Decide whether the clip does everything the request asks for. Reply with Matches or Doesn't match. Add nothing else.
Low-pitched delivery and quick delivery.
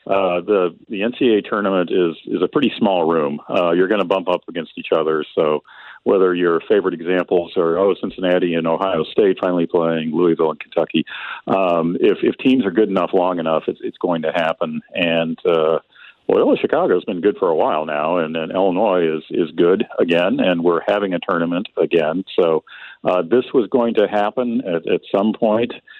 Doesn't match